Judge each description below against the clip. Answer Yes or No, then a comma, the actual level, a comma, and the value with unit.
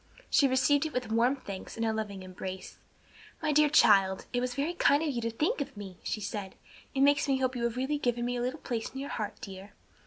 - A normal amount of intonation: Yes, average, 5.0 semitones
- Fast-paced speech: Yes, fast, 245 wpm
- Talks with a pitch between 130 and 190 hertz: No, high, 245 Hz